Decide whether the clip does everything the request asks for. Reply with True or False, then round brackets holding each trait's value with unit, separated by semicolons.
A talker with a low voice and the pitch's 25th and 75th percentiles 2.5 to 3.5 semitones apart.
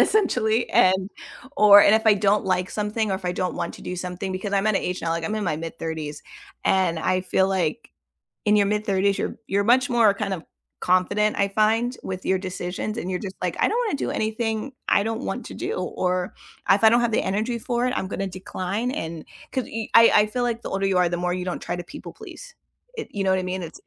False (195 Hz; 3.2 semitones)